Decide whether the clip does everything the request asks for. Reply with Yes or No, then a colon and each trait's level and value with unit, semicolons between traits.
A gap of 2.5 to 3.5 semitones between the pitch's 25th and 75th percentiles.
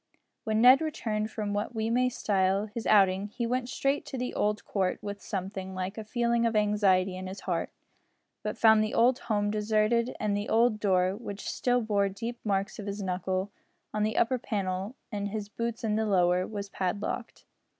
Yes: average, 2.8 semitones